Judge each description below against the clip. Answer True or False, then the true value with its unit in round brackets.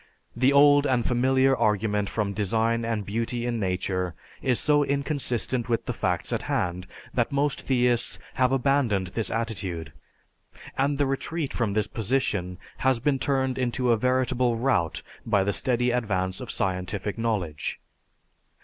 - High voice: False (120 Hz)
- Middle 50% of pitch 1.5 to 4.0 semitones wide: False (4.5 semitones)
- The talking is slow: False (150 wpm)